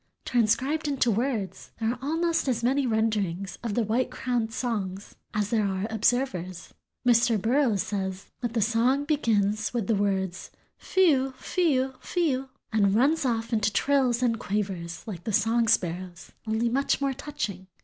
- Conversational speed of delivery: Yes, average, 165 wpm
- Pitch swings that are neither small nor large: Yes, average, 4.3 semitones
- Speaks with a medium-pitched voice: No, high, 230 Hz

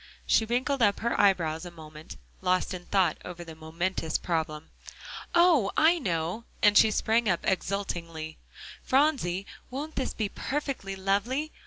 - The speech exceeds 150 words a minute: No, average, 145 wpm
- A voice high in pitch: Yes, high, 195 Hz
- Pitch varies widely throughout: Yes, wide, 6.1 semitones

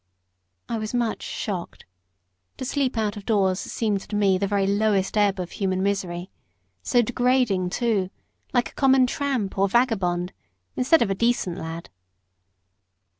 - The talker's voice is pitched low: No, high, 205 Hz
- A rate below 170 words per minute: Yes, average, 150 wpm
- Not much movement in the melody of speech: No, average, 4.1 semitones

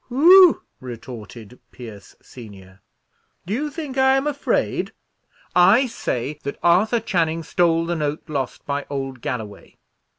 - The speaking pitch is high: No, medium, 160 Hz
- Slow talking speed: Yes, slow, 130 wpm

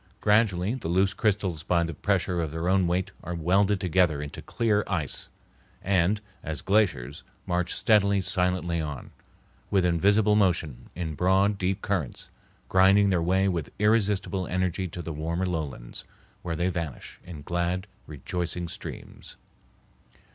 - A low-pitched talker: Yes, very low, 90 Hz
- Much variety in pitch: No, average, 2.7 semitones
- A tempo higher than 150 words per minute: No, average, 140 wpm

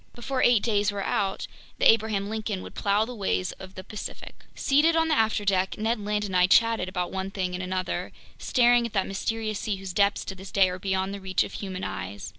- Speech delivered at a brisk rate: Yes, fast, 225 wpm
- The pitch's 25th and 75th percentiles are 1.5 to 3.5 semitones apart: Yes, average, 2.8 semitones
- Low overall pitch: No, high, 200 Hz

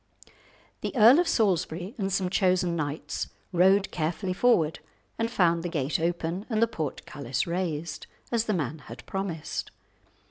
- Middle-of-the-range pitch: Yes, medium, 180 Hz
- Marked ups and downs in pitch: No, average, 3.7 semitones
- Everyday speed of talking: Yes, average, 145 wpm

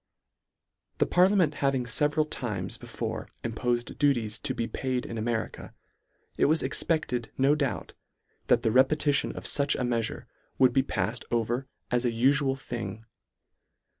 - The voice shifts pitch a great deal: No, average, 3.3 semitones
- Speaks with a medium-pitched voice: No, low, 125 Hz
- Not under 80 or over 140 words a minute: No, average, 150 wpm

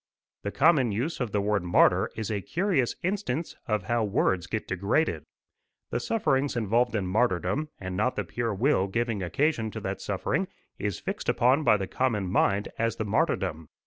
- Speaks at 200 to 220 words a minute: No, average, 175 wpm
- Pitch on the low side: Yes, low, 110 Hz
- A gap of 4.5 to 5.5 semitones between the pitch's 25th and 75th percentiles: Yes, average, 4.9 semitones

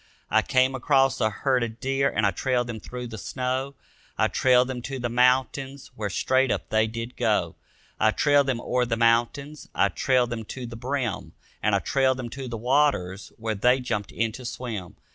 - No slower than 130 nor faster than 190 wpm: No, average, 200 wpm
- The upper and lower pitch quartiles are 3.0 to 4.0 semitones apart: No, narrow, 2.4 semitones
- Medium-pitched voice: No, low, 125 Hz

